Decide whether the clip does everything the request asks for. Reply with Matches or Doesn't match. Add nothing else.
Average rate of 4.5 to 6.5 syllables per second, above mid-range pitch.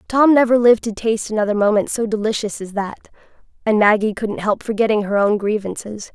Matches